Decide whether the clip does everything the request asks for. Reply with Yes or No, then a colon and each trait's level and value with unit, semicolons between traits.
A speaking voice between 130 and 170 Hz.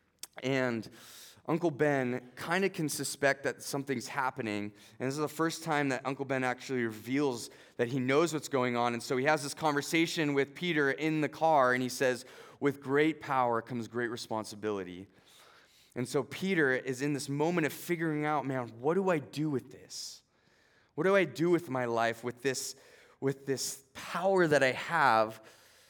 Yes: low, 135 Hz